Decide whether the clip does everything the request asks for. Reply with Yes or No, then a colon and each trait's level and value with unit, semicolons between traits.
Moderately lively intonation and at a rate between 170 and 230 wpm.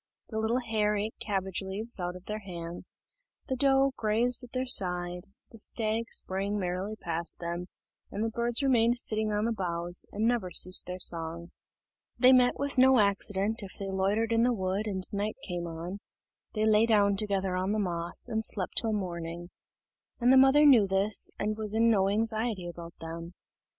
Yes: average, 3.8 semitones; average, 185 wpm